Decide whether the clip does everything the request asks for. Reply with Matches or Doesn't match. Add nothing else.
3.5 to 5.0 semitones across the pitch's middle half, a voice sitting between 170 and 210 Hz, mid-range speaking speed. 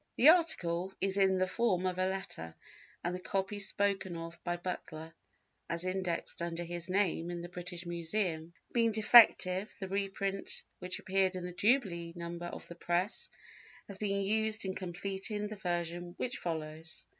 Doesn't match